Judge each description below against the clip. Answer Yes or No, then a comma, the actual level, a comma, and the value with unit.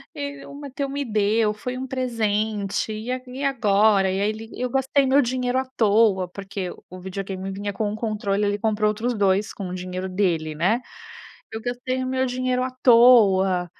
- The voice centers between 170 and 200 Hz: No, high, 215 Hz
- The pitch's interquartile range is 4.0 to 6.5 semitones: Yes, average, 4.3 semitones